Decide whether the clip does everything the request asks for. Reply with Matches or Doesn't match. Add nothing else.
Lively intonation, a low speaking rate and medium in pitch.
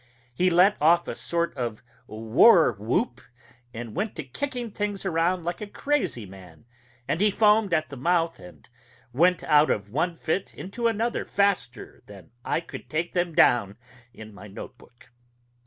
Doesn't match